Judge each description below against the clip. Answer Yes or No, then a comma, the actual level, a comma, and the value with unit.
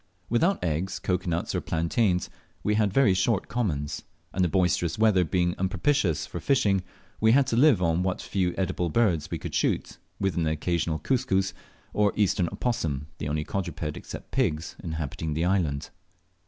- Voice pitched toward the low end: Yes, very low, 90 Hz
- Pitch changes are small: No, average, 4.2 semitones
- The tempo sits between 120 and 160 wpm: No, average, 170 wpm